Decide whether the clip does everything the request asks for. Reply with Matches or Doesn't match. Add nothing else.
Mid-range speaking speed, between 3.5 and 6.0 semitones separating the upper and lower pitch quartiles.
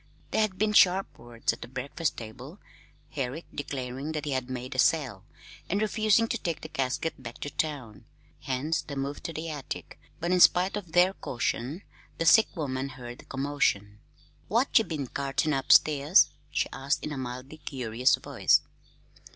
Matches